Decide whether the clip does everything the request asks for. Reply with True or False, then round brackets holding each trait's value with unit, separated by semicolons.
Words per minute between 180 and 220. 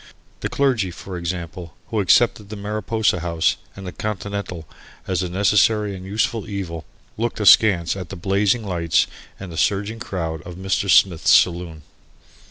False (155 wpm)